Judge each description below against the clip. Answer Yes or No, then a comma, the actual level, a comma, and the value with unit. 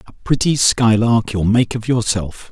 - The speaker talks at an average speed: Yes, average, 165 wpm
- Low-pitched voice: Yes, low, 115 Hz